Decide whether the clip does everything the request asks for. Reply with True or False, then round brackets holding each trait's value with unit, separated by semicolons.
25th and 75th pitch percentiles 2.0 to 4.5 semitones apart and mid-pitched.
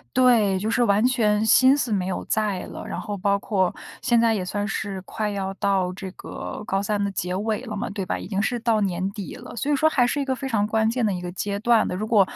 False (3.1 semitones; 210 Hz)